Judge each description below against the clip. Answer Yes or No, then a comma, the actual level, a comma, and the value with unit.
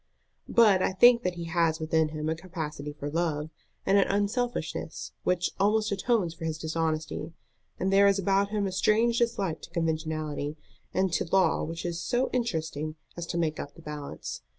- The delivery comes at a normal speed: Yes, average, 180 wpm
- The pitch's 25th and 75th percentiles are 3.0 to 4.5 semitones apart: Yes, average, 4.1 semitones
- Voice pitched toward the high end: No, medium, 170 Hz